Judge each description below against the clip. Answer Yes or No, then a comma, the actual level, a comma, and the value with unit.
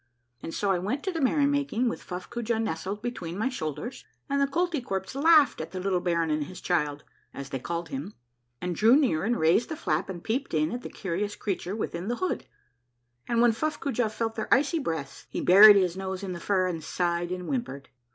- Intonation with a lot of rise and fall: Yes, wide, 6.1 semitones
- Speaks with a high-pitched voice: Yes, high, 195 Hz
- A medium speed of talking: No, fast, 220 wpm